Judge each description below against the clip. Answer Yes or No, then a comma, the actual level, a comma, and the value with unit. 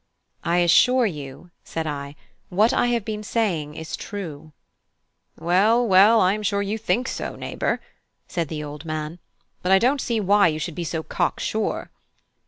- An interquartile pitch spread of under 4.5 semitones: No, average, 5.3 semitones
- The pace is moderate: Yes, average, 170 wpm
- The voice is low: No, medium, 180 Hz